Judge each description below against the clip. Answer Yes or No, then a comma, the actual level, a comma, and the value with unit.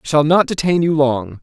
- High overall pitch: No, medium, 150 Hz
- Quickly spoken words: Yes, fast, 255 wpm